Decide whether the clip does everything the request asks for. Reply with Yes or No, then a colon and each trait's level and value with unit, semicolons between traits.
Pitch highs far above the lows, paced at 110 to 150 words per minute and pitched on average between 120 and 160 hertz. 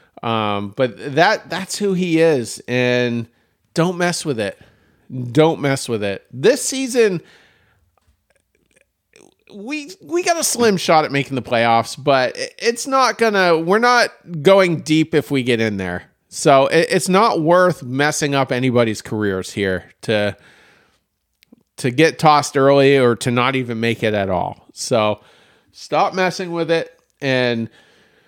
Yes: wide, 7.4 semitones; average, 140 wpm; medium, 140 Hz